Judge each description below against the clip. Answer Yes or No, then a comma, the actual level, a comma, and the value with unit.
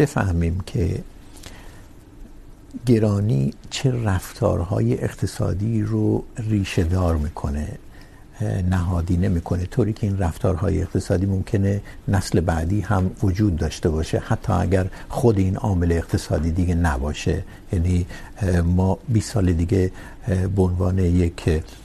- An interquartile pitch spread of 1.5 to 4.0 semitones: Yes, average, 2.8 semitones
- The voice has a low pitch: Yes, very low, 95 Hz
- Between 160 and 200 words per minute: No, slow, 100 wpm